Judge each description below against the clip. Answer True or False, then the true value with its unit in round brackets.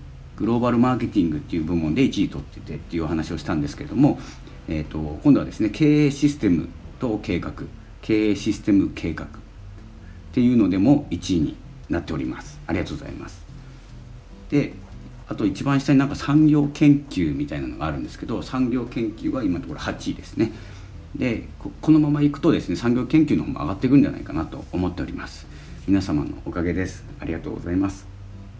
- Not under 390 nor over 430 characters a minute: True (395 characters per minute)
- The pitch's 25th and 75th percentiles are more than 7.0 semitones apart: True (7.9 semitones)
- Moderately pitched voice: False (110 Hz)